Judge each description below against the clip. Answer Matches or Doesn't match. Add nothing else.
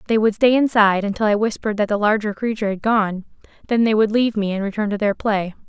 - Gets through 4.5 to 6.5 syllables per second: Doesn't match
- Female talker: Matches